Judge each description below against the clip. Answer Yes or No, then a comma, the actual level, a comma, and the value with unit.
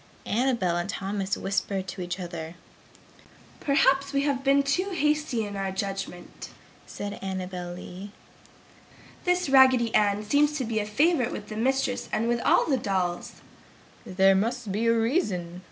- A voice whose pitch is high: Yes, high, 215 Hz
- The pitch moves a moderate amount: No, wide, 5.9 semitones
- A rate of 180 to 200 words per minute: No, average, 145 wpm